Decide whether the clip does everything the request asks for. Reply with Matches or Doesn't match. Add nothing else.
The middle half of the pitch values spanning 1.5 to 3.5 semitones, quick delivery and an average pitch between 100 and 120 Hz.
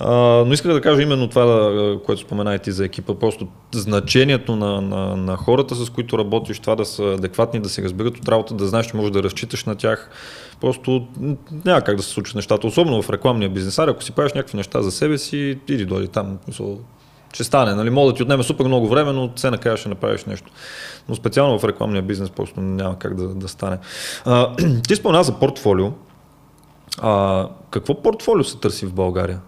Doesn't match